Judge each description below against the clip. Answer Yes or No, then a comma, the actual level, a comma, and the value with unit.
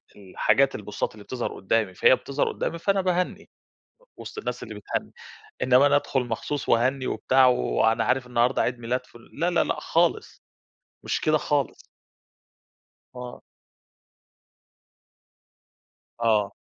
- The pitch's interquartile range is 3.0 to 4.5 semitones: Yes, average, 3.8 semitones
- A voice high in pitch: No, low, 125 Hz